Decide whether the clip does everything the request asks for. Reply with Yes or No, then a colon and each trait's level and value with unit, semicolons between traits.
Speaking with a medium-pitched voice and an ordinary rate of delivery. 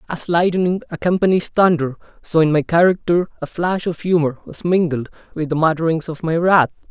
Yes: medium, 165 Hz; average, 175 wpm